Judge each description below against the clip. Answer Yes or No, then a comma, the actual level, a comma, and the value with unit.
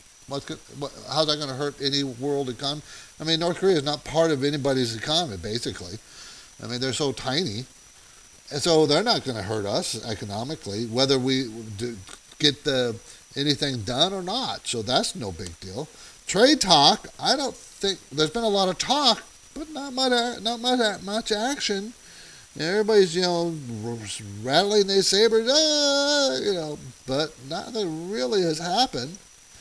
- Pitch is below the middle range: No, medium, 145 Hz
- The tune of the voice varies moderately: No, wide, 7.7 semitones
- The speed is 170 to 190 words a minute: No, average, 160 wpm